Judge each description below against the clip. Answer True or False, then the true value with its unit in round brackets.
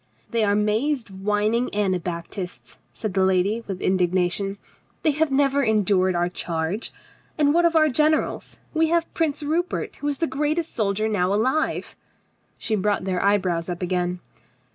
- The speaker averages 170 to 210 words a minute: False (155 wpm)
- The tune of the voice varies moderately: False (7.5 semitones)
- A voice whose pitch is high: True (210 Hz)